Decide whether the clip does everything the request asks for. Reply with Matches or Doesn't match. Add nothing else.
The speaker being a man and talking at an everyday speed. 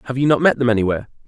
Doesn't match